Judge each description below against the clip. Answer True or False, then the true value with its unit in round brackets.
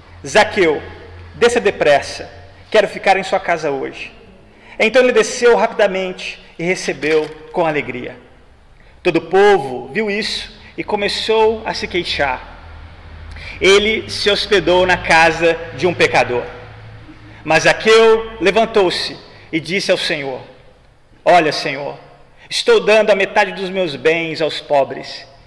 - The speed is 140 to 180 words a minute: False (125 wpm)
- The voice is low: False (180 Hz)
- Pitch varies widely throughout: True (6.1 semitones)